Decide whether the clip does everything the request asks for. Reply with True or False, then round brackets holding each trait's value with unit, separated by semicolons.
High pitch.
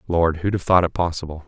False (85 Hz)